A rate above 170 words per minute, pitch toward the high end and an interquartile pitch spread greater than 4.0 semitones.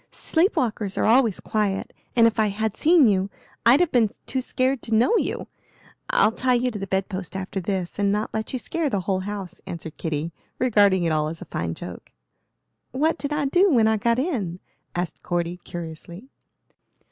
Yes: average, 195 wpm; high, 210 Hz; wide, 5.5 semitones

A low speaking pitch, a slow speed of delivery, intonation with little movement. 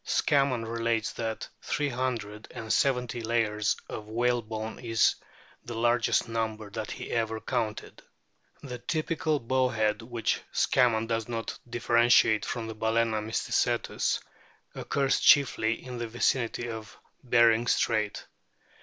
Yes: low, 115 Hz; slow, 125 wpm; narrow, 1.7 semitones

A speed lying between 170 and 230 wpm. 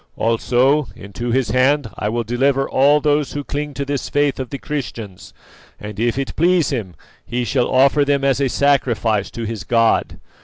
Yes: average, 185 wpm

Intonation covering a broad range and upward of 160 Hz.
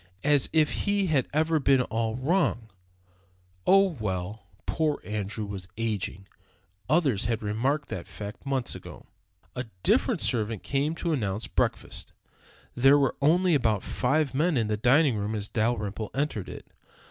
No: wide, 5.9 semitones; low, 125 Hz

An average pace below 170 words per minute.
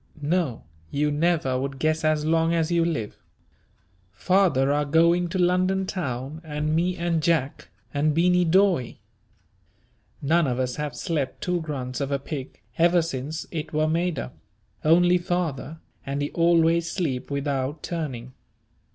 Yes: average, 150 wpm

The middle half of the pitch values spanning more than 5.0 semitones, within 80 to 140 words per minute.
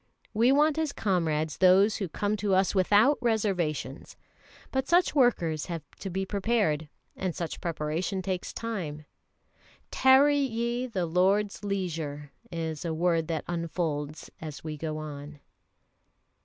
Yes: wide, 5.4 semitones; slow, 135 wpm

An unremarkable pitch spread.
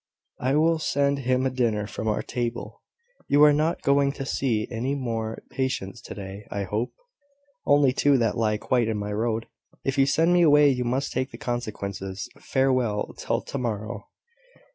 Yes: average, 4.3 semitones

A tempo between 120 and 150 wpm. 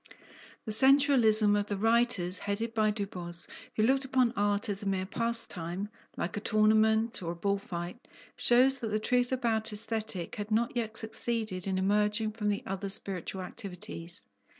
No: average, 170 wpm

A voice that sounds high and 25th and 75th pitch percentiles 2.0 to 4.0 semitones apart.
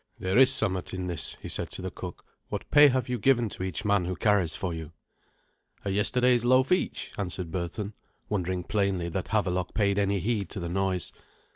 No: low, 100 Hz; average, 3.4 semitones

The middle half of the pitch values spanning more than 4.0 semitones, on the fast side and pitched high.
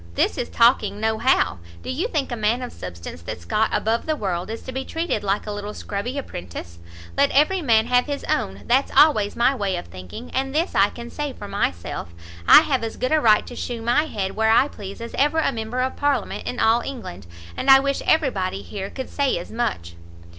Yes: average, 5.1 semitones; fast, 225 wpm; high, 235 Hz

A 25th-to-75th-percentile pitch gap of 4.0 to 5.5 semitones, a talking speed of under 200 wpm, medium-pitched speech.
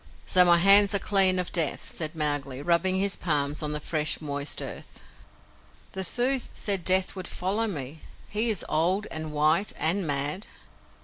Yes: average, 4.4 semitones; average, 170 wpm; medium, 175 Hz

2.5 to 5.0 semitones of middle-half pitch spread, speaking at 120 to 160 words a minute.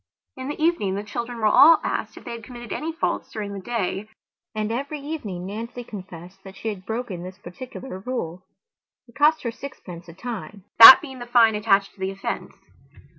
No: average, 4.5 semitones; average, 195 wpm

